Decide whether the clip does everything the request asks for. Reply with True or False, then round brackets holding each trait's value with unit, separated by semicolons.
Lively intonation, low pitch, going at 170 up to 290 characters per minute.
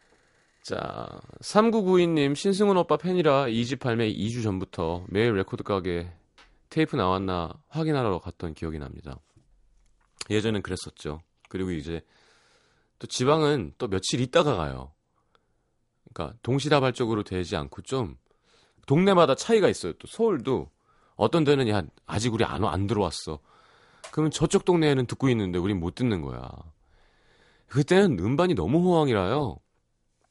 True (8.8 semitones; 110 Hz; 280 characters per minute)